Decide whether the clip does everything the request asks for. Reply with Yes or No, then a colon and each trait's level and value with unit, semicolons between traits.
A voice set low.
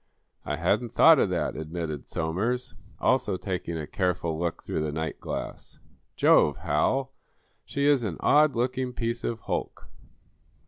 Yes: very low, 95 Hz